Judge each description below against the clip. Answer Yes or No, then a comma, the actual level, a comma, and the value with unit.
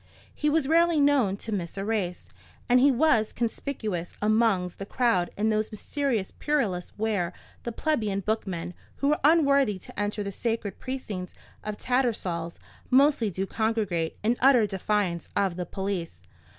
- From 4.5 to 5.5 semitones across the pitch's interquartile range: Yes, average, 5.1 semitones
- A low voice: No, high, 215 Hz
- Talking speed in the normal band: Yes, average, 150 wpm